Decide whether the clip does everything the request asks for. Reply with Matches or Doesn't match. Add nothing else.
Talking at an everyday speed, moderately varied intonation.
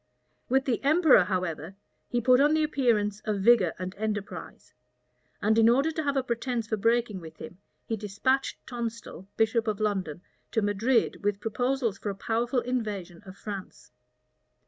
Matches